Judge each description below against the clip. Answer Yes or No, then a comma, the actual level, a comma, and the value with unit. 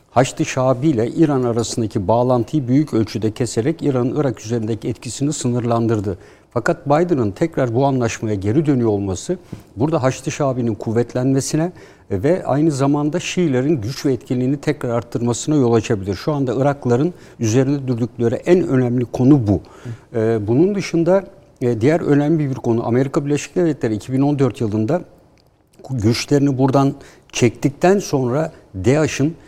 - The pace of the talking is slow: No, average, 125 wpm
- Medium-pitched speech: No, low, 130 Hz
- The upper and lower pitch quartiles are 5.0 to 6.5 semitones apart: No, average, 4.2 semitones